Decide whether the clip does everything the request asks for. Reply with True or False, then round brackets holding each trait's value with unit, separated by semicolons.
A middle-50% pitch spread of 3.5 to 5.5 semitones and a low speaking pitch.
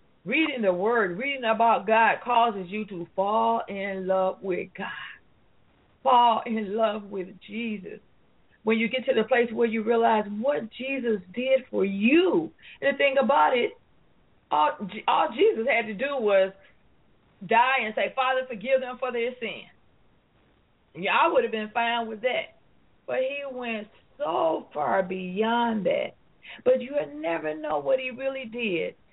False (4.2 semitones; 230 Hz)